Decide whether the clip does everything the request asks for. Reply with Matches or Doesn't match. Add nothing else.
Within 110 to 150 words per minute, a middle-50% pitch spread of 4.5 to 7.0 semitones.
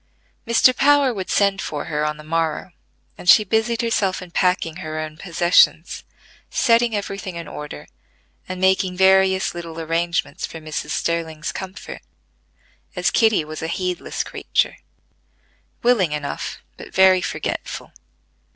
Doesn't match